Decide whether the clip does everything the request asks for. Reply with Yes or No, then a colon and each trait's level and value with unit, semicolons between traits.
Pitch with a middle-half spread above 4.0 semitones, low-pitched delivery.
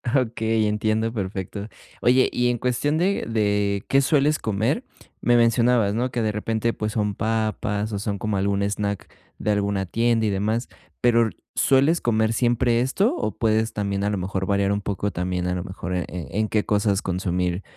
No: average, 2.7 semitones; low, 110 Hz